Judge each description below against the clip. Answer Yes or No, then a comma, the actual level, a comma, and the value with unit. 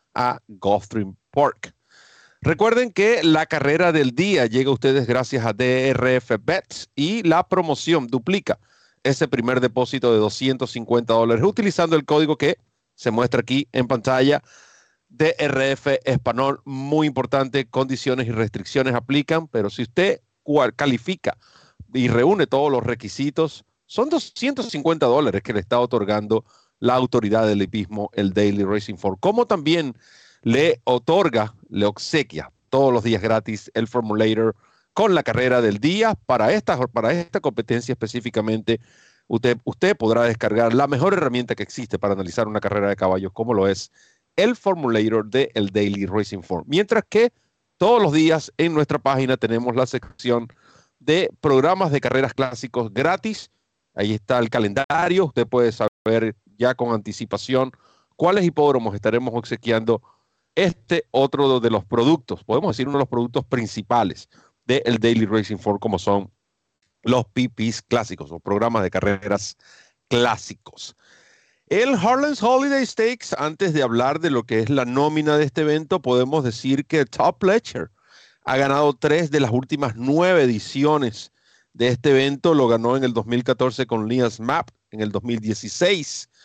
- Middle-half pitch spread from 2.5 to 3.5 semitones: No, average, 4.7 semitones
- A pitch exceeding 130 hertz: No, low, 125 Hz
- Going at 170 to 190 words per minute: No, average, 150 wpm